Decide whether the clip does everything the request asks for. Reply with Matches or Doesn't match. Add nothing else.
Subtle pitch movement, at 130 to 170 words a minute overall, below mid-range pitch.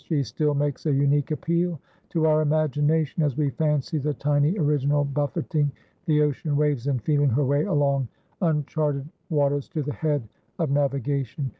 Doesn't match